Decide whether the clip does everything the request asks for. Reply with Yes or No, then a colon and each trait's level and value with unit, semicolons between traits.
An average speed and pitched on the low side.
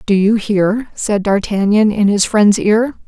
No: average, 175 wpm; high, 210 Hz